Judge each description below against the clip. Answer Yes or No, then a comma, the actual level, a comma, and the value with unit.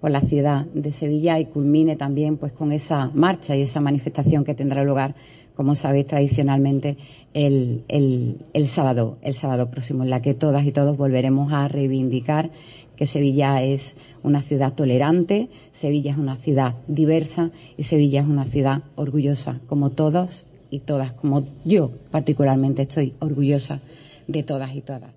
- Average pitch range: No, narrow, 1.6 semitones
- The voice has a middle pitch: Yes, medium, 145 Hz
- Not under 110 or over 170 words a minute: Yes, average, 160 wpm